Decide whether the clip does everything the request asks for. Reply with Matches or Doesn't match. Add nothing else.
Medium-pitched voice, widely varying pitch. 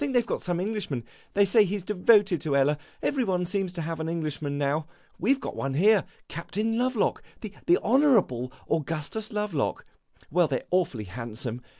Matches